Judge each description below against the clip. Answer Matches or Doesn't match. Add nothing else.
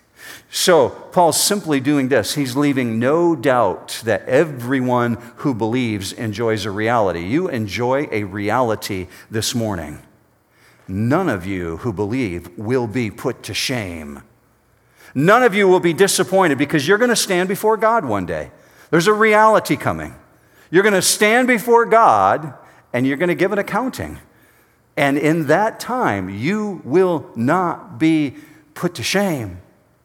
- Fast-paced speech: Doesn't match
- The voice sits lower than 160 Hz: Matches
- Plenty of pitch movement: Matches